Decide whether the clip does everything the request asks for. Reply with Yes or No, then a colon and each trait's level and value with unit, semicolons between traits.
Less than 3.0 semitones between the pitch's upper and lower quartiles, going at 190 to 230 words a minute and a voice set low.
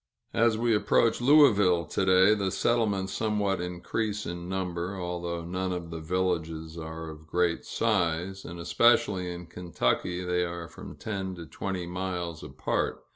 No: narrow, 2.5 semitones; average, 150 wpm; very low, 90 Hz